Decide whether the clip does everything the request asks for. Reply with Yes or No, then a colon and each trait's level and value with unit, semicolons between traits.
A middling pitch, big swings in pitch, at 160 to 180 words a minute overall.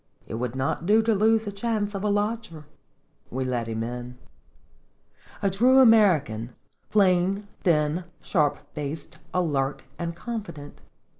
No: medium, 175 Hz; wide, 7.4 semitones; slow, 135 wpm